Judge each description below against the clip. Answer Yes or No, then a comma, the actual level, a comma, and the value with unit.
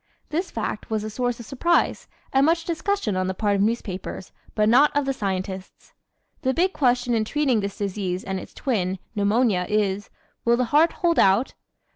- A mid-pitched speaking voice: No, high, 225 Hz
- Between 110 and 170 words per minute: No, average, 185 wpm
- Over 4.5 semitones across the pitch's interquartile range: Yes, wide, 5.4 semitones